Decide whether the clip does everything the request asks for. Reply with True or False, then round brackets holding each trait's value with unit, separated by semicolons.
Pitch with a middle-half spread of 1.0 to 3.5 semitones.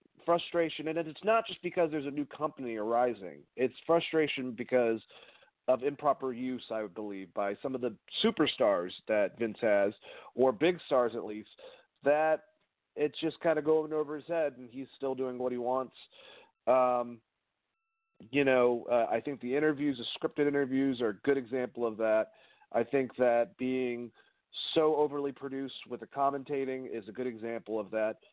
False (4.2 semitones)